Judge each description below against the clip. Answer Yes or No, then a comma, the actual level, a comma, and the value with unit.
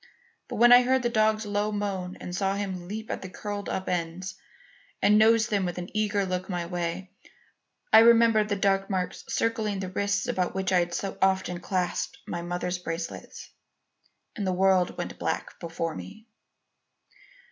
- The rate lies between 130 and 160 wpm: No, average, 175 wpm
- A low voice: No, high, 190 Hz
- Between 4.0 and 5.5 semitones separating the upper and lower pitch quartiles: No, average, 2.9 semitones